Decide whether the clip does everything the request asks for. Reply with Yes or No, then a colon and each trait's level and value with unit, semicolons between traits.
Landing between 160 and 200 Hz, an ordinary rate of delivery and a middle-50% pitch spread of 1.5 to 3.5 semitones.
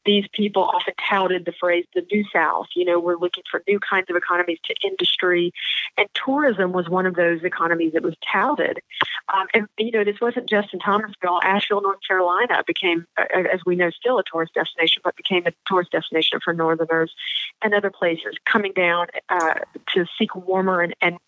Yes: medium, 185 Hz; average, 190 wpm; average, 2.9 semitones